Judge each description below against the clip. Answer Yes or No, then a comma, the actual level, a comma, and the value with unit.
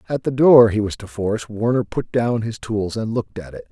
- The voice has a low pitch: Yes, low, 110 Hz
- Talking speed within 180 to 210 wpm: No, fast, 260 wpm